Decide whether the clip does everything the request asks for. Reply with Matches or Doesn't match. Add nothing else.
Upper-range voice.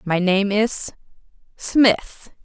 Matches